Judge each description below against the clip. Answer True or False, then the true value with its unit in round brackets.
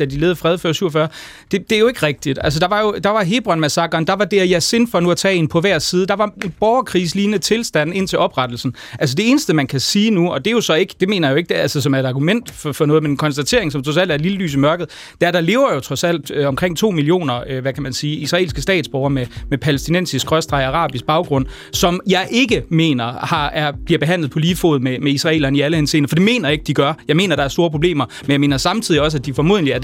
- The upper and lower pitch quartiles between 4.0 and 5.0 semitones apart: True (4.6 semitones)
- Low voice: False (160 Hz)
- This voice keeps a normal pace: False (290 wpm)